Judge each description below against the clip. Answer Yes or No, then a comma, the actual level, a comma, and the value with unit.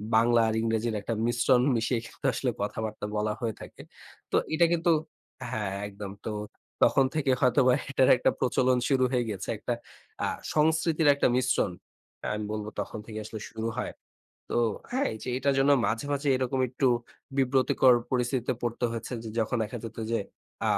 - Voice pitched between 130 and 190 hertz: No, low, 120 Hz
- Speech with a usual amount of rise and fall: Yes, average, 3.1 semitones